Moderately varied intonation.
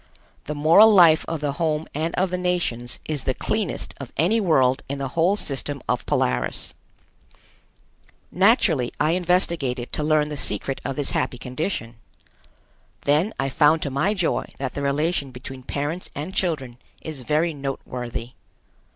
Yes: average, 4.2 semitones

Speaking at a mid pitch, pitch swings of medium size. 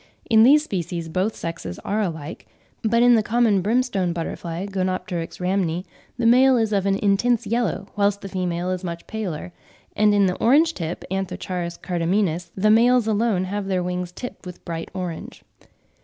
No: high, 195 Hz; average, 3.8 semitones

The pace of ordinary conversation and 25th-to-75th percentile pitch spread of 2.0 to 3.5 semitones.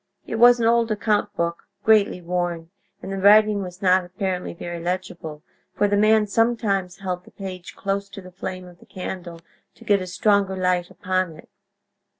Yes: average, 180 wpm; narrow, 2.5 semitones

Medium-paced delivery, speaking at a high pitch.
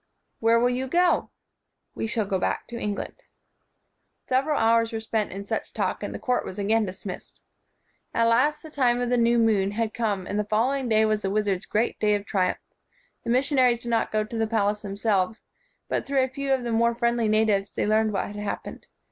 No: fast, 235 wpm; high, 225 Hz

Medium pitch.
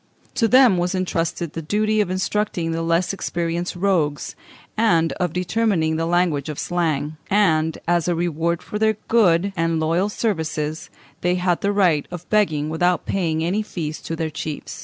Yes: medium, 175 Hz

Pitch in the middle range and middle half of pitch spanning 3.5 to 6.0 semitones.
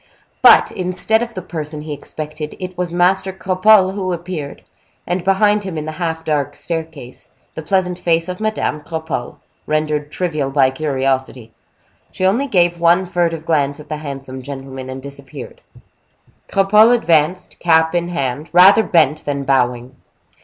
Yes: medium, 160 Hz; average, 4.2 semitones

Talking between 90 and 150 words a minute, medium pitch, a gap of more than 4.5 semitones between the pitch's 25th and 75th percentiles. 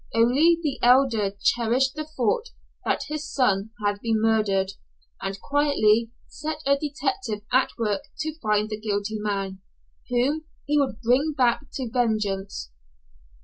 No: average, 140 wpm; high, 235 Hz; average, 5.0 semitones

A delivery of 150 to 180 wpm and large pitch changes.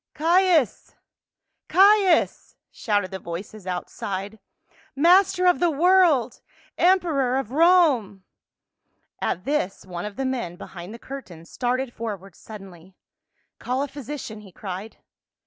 No: average, 140 wpm; wide, 8.9 semitones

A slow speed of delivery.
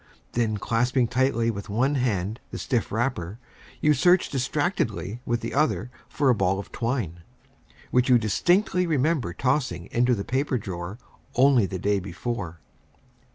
No: average, 150 wpm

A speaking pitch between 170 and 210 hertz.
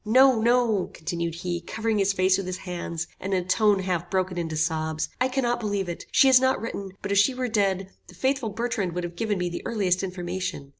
Yes: high, 190 Hz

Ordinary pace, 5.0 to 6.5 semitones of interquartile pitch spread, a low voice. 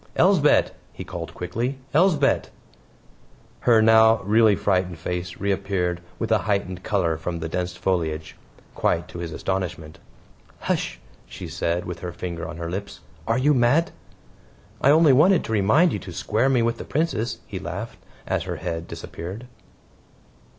Yes: average, 155 wpm; wide, 5.5 semitones; low, 100 Hz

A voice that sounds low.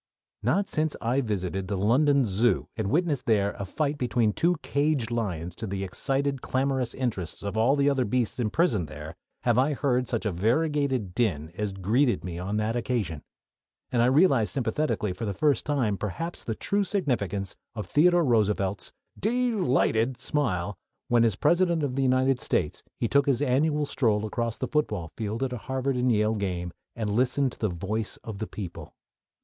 Yes: low, 120 Hz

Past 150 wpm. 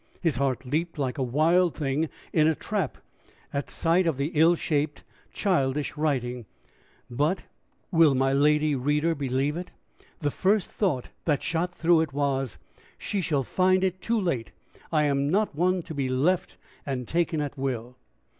Yes: average, 165 wpm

